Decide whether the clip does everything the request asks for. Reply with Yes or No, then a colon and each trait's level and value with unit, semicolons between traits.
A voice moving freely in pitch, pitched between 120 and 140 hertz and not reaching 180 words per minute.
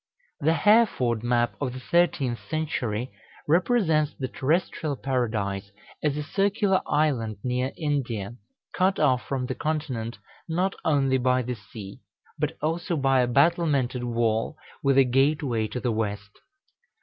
No: average, 4.6 semitones; low, 135 Hz; slow, 135 wpm